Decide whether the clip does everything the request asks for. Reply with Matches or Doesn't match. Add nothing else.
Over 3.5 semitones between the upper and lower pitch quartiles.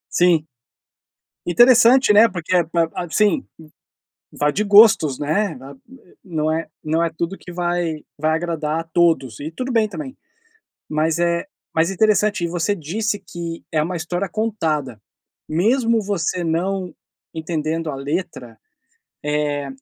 Matches